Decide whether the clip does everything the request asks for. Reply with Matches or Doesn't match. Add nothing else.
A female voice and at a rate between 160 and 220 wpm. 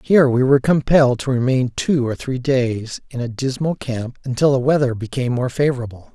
Doesn't match